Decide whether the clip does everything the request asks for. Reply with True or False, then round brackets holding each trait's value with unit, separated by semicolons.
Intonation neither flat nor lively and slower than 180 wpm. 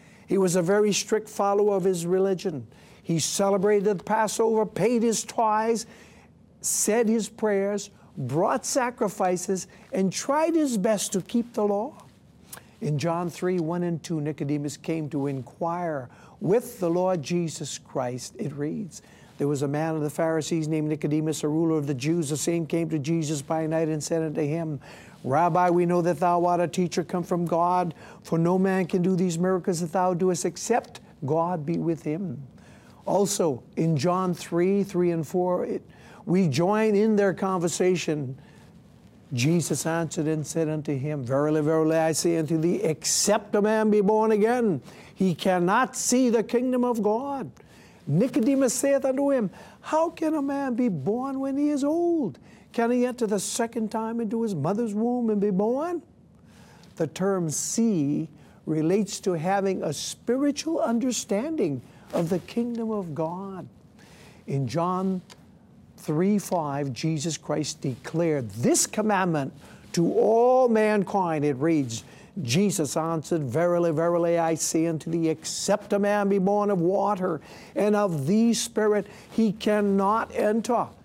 True (4.9 semitones; 155 wpm)